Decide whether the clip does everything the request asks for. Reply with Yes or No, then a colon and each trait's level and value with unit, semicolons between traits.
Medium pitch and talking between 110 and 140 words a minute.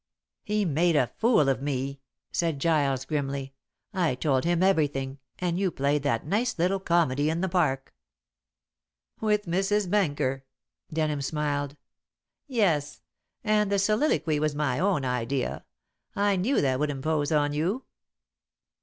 Yes: medium, 155 Hz; slow, 135 wpm